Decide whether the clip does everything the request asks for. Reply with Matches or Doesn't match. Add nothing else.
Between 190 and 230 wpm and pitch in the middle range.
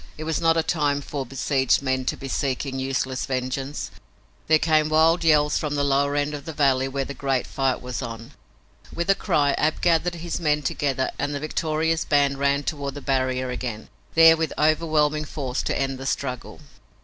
Matches